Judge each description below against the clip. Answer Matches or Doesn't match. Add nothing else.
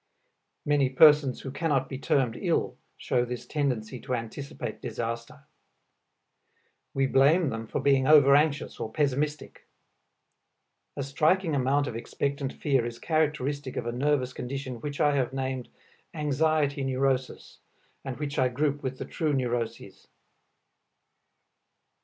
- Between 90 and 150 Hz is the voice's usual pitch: Matches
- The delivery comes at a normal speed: Doesn't match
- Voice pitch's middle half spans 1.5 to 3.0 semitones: Matches